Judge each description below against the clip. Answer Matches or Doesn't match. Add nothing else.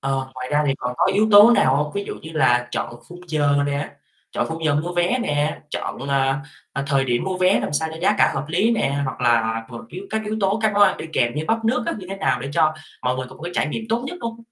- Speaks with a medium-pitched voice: Matches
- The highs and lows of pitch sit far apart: Matches